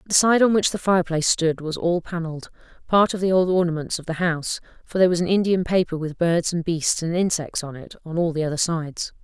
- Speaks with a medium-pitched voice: Yes, medium, 170 Hz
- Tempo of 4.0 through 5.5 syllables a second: No, 6.1 syllables/s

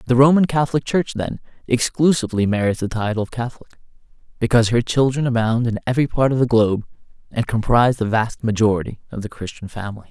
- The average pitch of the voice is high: No, low, 120 Hz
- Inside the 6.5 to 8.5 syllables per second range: Yes, 6.6 syllables/s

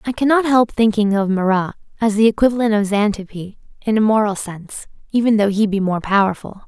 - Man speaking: No, female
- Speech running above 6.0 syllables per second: No, 4.9 syllables/s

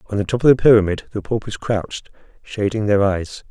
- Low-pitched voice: Yes, low, 105 Hz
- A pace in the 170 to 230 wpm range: Yes, fast, 205 wpm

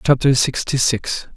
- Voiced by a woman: No, male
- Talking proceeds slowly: Yes, slow, 130 wpm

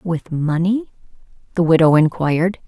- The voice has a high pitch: No, medium, 170 Hz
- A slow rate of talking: Yes, slow, 110 wpm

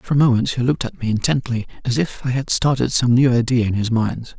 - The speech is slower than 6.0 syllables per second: No, 6.1 syllables/s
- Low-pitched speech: Yes, low, 125 Hz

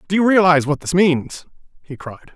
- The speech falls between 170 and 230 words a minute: Yes, fast, 205 wpm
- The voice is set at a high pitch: No, medium, 170 Hz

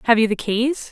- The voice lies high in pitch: Yes, high, 235 Hz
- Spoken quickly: Yes, fast, 265 wpm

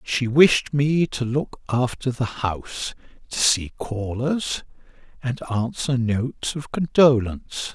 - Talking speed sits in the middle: No, slow, 125 wpm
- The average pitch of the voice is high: No, low, 125 Hz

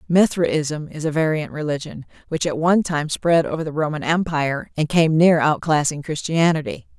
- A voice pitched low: No, medium, 155 Hz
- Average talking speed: Yes, average, 165 wpm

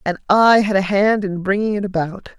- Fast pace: Yes, fast, 225 wpm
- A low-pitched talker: No, high, 200 Hz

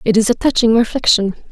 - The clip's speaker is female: Yes, female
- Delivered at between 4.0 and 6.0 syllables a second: No, 6.2 syllables/s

